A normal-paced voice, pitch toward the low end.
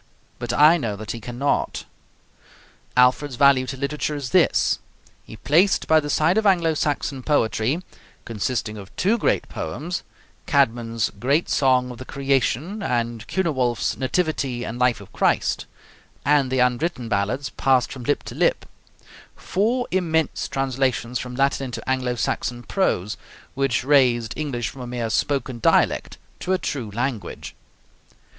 Yes: average, 145 wpm; low, 130 Hz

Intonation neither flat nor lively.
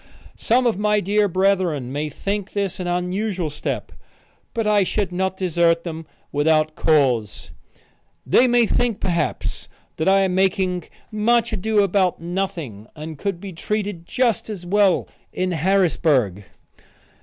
Yes: average, 4.0 semitones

